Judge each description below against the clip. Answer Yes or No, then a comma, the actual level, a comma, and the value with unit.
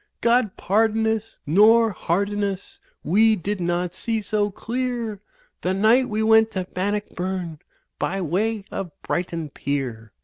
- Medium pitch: No, high, 205 Hz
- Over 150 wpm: No, slow, 135 wpm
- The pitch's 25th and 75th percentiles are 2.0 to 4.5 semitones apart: Yes, average, 3.6 semitones